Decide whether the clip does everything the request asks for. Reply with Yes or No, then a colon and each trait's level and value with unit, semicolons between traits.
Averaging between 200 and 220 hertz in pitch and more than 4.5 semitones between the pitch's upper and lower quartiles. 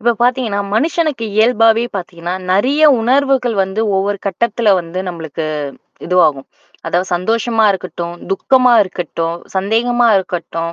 Yes: high, 205 Hz; average, 5.3 semitones